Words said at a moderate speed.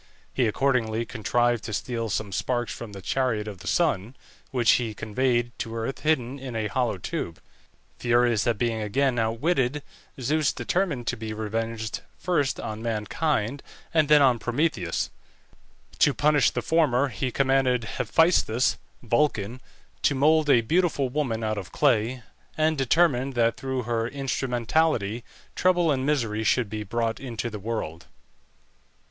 Yes: average, 145 wpm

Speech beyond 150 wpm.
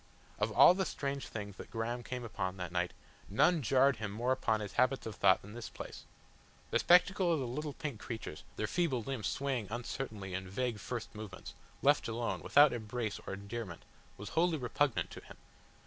Yes: average, 185 wpm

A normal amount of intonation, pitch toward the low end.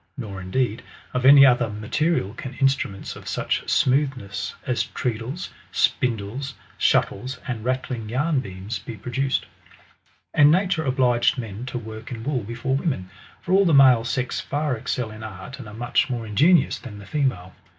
Yes: average, 3.9 semitones; low, 125 Hz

